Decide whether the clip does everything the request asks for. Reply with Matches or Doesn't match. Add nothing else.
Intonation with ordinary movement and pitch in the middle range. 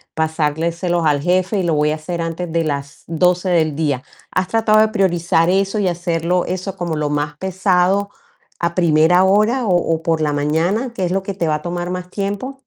Matches